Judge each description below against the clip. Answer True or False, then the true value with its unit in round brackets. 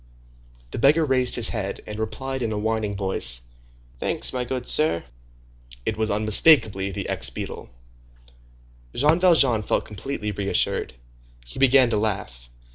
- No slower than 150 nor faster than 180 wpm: False (140 wpm)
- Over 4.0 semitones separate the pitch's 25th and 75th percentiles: True (4.6 semitones)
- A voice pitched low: True (110 Hz)